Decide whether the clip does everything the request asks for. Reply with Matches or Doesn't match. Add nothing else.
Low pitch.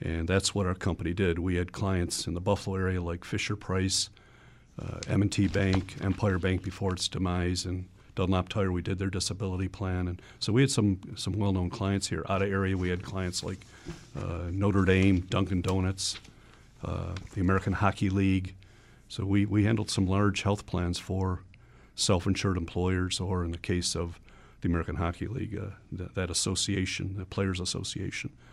Matches